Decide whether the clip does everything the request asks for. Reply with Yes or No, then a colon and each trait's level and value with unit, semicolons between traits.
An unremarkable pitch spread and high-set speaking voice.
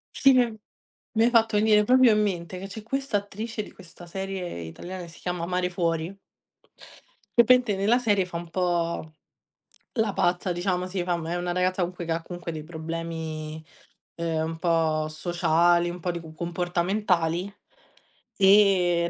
No: average, 3.0 semitones; medium, 180 Hz